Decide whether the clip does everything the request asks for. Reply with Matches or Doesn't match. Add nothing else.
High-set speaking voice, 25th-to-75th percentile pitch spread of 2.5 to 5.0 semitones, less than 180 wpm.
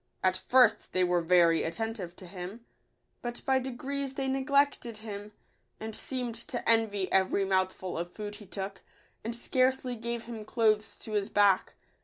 Matches